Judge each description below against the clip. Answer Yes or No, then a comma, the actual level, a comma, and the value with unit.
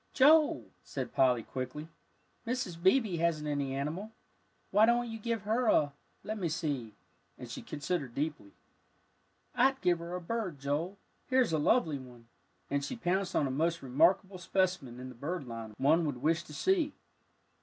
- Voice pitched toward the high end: No, medium, 165 Hz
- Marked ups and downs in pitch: Yes, wide, 6.9 semitones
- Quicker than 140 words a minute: Yes, average, 165 wpm